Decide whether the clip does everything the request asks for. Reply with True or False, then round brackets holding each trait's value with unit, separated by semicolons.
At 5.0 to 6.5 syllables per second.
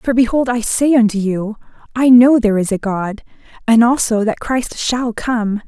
False (4.6 syllables/s)